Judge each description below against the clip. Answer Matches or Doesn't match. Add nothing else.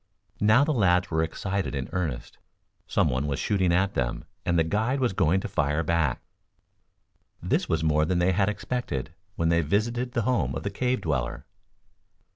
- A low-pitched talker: Matches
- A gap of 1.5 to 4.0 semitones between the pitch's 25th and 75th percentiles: Doesn't match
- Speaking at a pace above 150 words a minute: Matches